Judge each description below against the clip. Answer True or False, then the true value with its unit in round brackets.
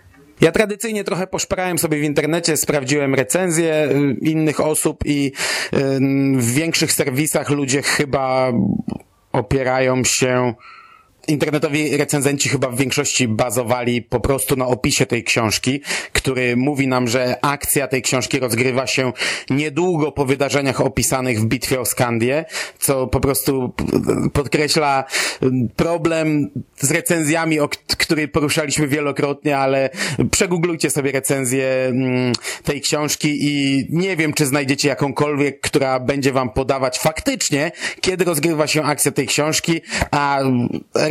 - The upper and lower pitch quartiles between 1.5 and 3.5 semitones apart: True (2.9 semitones)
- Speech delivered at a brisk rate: False (120 wpm)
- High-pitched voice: False (145 Hz)